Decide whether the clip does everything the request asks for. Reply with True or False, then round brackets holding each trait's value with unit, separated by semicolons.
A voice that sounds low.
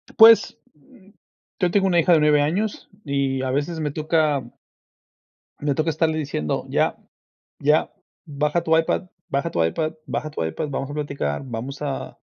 False (150 Hz)